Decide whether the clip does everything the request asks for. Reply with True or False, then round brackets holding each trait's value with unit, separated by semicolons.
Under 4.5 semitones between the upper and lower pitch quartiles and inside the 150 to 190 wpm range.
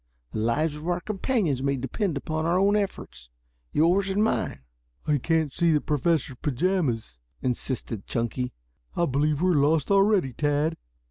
False (5.1 semitones; 155 wpm)